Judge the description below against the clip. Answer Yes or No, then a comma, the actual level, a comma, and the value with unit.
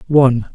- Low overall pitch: Yes, low, 130 Hz